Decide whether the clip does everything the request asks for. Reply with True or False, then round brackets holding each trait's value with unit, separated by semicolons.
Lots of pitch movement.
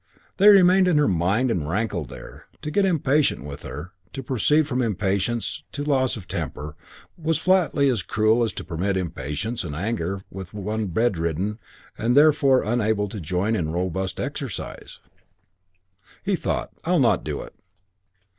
True (6.8 semitones)